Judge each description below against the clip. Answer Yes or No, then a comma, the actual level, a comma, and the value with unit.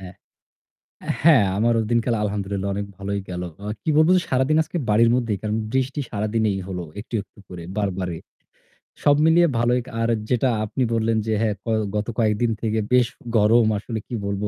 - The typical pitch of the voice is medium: No, low, 110 Hz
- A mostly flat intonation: No, average, 3.6 semitones